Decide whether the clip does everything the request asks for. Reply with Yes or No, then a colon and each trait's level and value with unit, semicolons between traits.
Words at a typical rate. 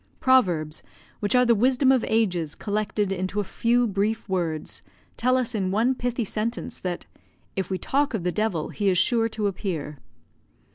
Yes: average, 175 wpm